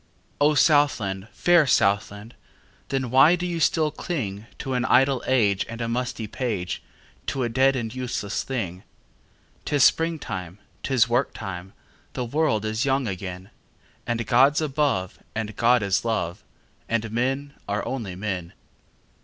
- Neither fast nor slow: No, slow, 120 wpm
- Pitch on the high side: No, low, 120 Hz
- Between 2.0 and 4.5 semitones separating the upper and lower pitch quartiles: No, average, 5.0 semitones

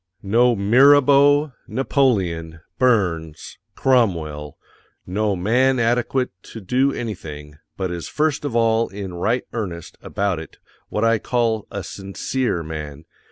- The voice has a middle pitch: No, low, 110 Hz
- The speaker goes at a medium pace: No, slow, 120 wpm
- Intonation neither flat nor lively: No, wide, 6.4 semitones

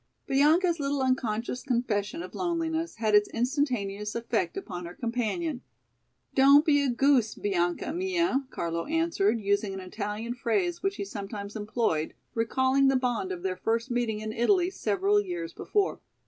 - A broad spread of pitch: Yes, wide, 7.4 semitones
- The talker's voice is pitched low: No, high, 245 Hz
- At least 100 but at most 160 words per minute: Yes, average, 150 wpm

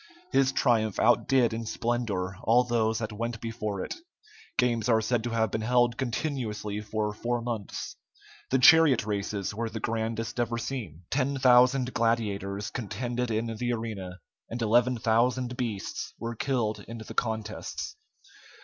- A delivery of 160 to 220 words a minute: No, average, 150 wpm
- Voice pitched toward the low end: Yes, low, 115 Hz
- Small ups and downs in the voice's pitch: Yes, narrow, 2.1 semitones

